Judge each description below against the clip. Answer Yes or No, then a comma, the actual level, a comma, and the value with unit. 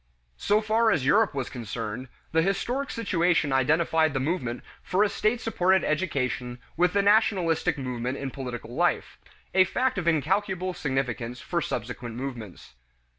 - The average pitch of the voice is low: No, medium, 160 Hz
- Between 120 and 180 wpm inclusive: Yes, average, 145 wpm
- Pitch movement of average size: No, wide, 7.0 semitones